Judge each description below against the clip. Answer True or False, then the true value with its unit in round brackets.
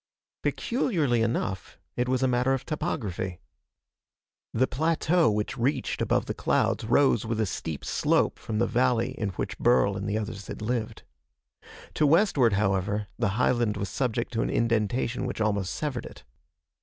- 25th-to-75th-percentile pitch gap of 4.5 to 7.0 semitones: False (3.6 semitones)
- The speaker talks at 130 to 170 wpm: True (160 wpm)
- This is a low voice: True (115 Hz)